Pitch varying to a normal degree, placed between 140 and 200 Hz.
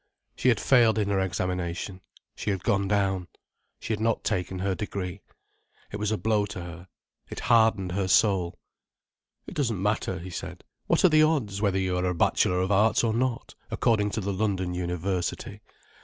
No: average, 3.1 semitones; low, 100 Hz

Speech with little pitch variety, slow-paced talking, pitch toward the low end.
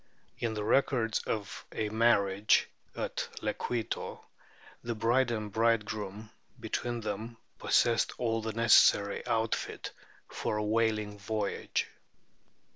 Yes: narrow, 1.6 semitones; slow, 120 wpm; low, 110 Hz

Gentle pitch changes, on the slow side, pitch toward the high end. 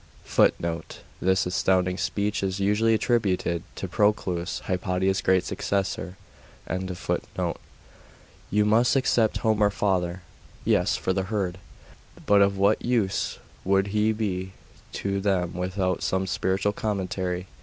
No: narrow, 2.0 semitones; slow, 115 wpm; very low, 95 Hz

